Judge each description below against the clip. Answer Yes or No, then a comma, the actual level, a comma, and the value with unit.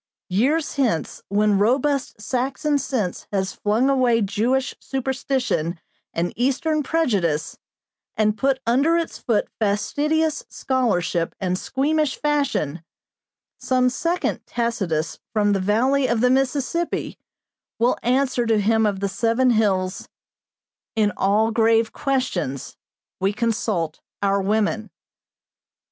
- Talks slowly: Yes, slow, 115 wpm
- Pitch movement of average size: Yes, average, 4.9 semitones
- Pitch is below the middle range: No, high, 230 Hz